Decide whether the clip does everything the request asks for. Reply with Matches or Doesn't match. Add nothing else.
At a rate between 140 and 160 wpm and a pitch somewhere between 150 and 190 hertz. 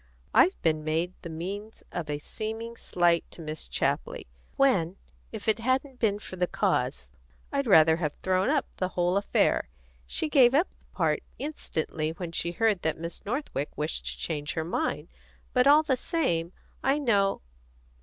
Doesn't match